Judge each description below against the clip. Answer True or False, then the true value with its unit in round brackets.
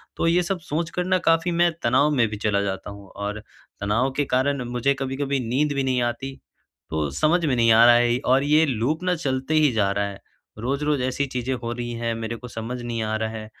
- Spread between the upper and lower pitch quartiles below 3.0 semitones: False (4.3 semitones)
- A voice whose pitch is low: True (125 Hz)